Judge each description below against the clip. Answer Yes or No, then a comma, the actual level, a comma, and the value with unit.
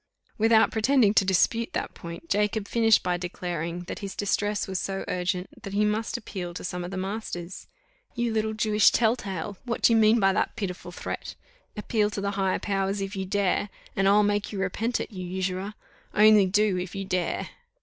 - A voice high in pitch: Yes, high, 200 Hz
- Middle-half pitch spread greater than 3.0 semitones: No, narrow, 2.6 semitones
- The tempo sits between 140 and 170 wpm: No, average, 200 wpm